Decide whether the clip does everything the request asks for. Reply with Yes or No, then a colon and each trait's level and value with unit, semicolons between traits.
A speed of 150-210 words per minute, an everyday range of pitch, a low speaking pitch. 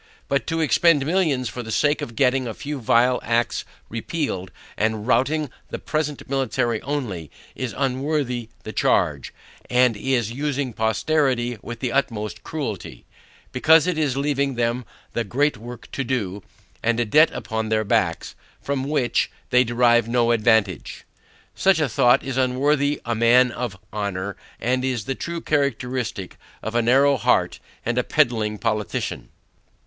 Yes: average, 155 wpm; average, 3.5 semitones; low, 125 Hz